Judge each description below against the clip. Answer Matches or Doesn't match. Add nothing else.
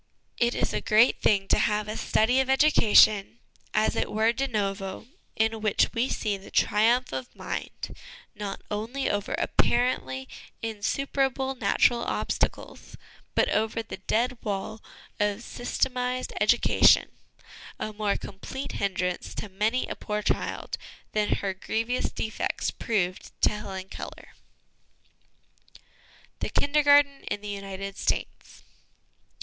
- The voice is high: Matches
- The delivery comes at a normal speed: Doesn't match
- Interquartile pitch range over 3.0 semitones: Matches